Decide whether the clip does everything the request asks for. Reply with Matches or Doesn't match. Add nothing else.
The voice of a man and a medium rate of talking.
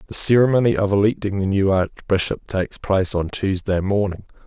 Matches